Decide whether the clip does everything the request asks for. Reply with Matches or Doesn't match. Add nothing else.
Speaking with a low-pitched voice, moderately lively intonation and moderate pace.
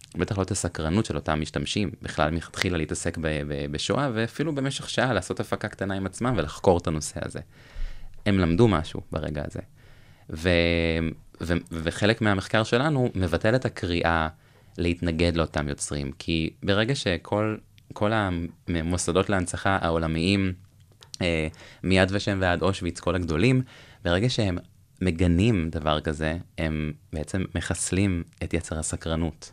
Matches